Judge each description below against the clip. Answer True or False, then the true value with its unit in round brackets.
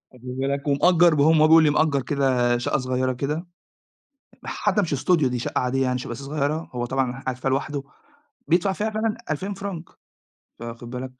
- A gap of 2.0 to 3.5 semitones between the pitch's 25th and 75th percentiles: False (4.0 semitones)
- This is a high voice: False (140 Hz)